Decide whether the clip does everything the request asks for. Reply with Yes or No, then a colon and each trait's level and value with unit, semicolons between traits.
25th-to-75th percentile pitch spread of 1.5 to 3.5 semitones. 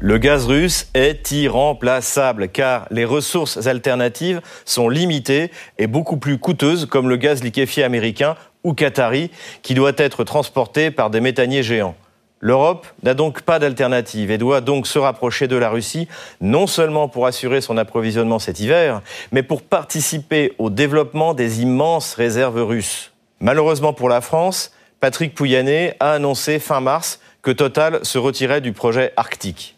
No: average, 4.1 semitones